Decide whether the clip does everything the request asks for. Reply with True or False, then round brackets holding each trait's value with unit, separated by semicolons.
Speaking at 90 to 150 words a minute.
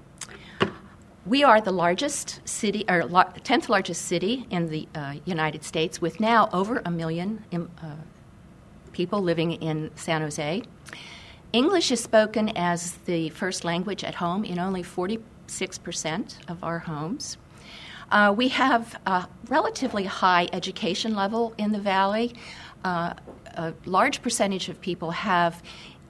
True (135 wpm)